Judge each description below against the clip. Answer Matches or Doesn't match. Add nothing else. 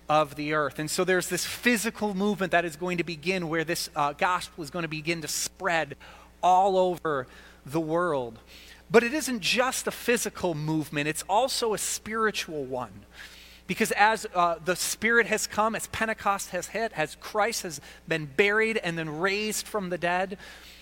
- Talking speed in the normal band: Matches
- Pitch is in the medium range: Matches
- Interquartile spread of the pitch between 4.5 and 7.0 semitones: Matches